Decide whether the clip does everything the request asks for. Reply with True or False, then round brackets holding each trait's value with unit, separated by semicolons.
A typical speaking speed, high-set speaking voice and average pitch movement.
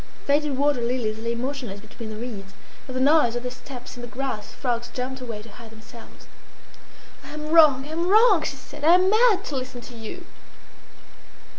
True (195 wpm; 255 Hz; 4.1 semitones)